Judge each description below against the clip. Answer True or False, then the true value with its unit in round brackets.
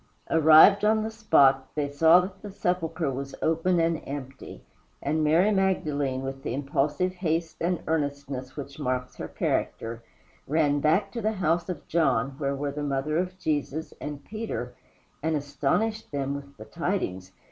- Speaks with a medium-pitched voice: True (150 Hz)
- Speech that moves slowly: False (160 wpm)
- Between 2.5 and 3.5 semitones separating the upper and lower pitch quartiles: False (4.4 semitones)